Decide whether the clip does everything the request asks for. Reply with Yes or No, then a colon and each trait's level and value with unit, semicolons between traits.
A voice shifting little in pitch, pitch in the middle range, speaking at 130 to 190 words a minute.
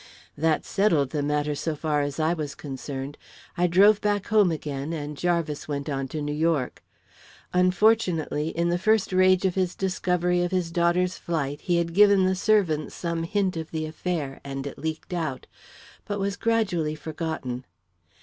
No: average, 3.8 semitones; medium, 165 Hz; average, 170 wpm